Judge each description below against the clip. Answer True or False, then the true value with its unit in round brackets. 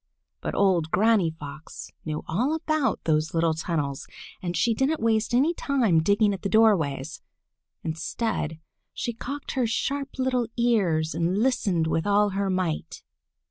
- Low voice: False (200 Hz)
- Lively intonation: True (6.6 semitones)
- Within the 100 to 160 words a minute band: True (145 wpm)